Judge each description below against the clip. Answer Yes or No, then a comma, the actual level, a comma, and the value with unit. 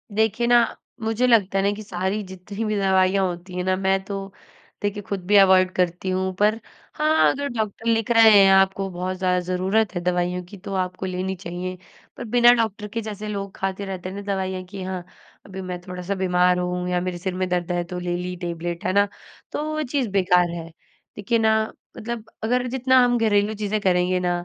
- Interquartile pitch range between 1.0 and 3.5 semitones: Yes, average, 2.9 semitones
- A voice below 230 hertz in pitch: Yes, high, 190 Hz